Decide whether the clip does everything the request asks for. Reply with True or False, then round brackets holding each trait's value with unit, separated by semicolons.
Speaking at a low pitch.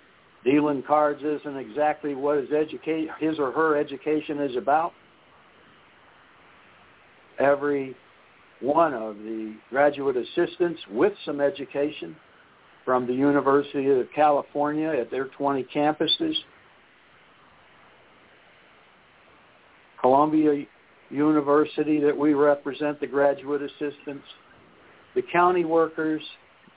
False (145 Hz)